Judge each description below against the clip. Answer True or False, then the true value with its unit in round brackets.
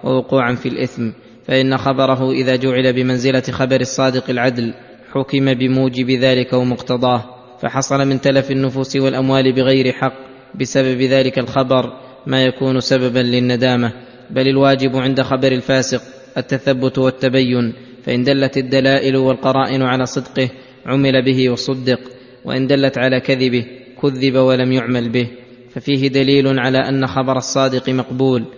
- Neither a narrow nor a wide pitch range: False (0.8 semitones)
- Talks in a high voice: False (130 Hz)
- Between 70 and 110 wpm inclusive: False (125 wpm)